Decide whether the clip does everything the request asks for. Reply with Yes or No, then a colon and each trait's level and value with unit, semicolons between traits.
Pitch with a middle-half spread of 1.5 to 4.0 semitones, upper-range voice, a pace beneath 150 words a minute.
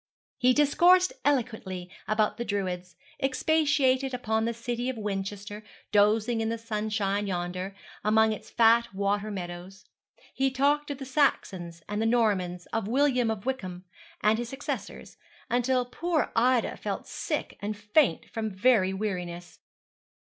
No: average, 4.4 semitones; high, 220 Hz; average, 140 wpm